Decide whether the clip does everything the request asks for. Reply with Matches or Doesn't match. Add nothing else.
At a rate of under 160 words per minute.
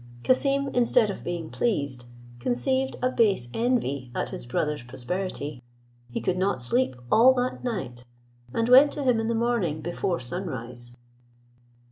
Matches